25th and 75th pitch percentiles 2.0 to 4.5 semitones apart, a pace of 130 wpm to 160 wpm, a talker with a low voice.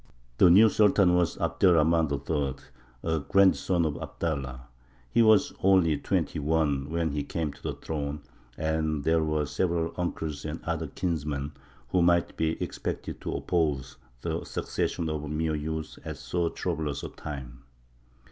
Yes: narrow, 2.6 semitones; average, 155 wpm; very low, 80 Hz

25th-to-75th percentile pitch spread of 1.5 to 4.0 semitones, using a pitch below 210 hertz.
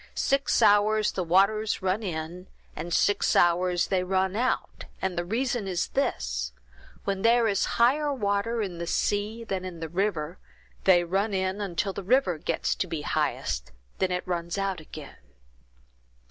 Yes: average, 3.4 semitones; high, 190 Hz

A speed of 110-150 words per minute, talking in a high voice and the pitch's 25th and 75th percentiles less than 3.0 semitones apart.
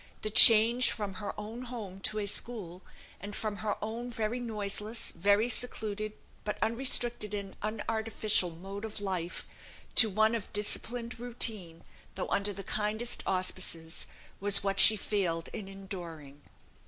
Yes: average, 140 wpm; high, 210 Hz; narrow, 2.5 semitones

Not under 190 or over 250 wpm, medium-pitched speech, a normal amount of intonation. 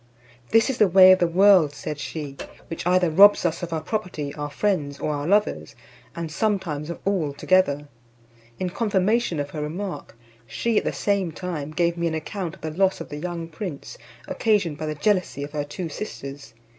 Yes: average, 200 wpm; medium, 170 Hz; average, 4.3 semitones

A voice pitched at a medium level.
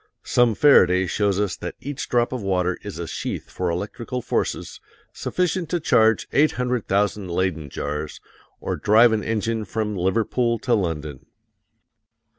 No: low, 105 Hz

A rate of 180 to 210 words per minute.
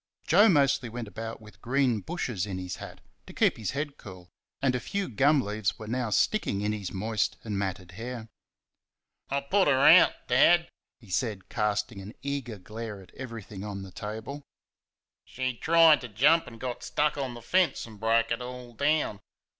Yes: average, 185 wpm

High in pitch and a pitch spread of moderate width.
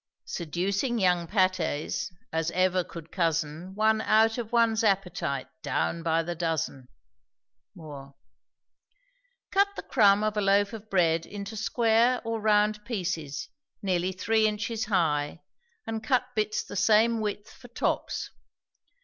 Yes: high, 200 Hz; average, 4.7 semitones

